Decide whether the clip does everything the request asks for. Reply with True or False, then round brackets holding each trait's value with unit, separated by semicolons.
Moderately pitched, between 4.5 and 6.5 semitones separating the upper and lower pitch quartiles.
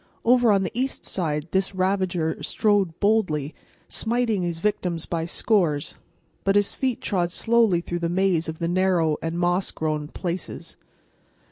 False (180 Hz; 3.7 semitones)